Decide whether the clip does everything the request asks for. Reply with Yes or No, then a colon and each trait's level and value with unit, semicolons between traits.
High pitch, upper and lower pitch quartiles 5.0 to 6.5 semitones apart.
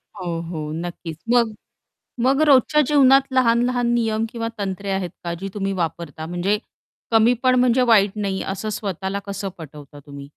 Yes: high, 200 Hz; wide, 5.5 semitones